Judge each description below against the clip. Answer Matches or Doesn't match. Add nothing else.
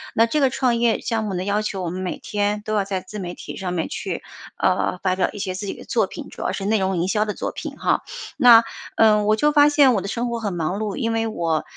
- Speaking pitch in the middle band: Doesn't match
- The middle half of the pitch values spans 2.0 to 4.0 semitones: Matches